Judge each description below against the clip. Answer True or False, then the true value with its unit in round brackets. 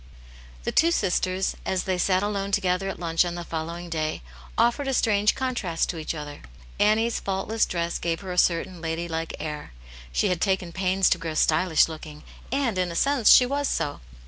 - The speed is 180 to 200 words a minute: True (195 wpm)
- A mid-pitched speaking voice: True (180 Hz)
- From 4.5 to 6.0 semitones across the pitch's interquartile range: False (3.7 semitones)